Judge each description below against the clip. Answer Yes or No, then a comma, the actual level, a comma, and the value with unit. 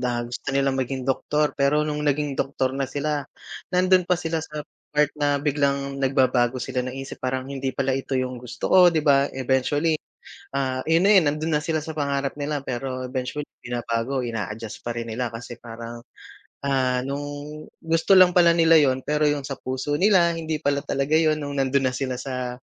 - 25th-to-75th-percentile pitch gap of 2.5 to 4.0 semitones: Yes, average, 2.8 semitones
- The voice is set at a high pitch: No, medium, 140 Hz